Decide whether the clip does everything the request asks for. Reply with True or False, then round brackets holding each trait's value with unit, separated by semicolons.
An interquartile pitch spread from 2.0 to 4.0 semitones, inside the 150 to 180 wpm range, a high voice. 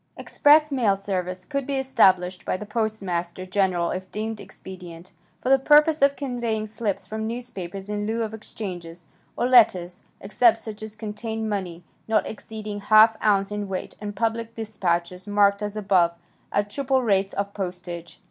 True (3.2 semitones; 160 wpm; 210 Hz)